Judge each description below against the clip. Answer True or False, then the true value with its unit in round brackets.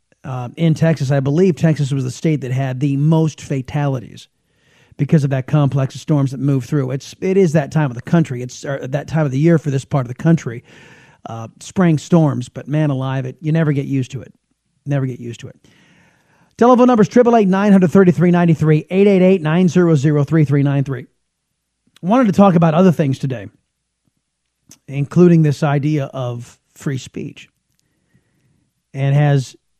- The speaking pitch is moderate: True (145 Hz)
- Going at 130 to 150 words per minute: False (195 wpm)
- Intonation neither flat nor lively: True (3.8 semitones)